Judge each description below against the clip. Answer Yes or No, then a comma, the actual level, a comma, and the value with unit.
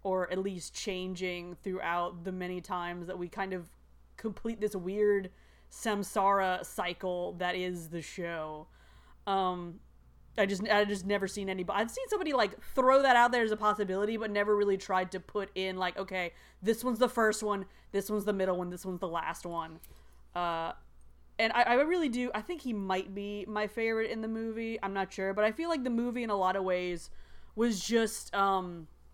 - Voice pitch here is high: Yes, high, 195 Hz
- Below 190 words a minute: No, average, 200 wpm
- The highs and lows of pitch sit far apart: No, average, 3.1 semitones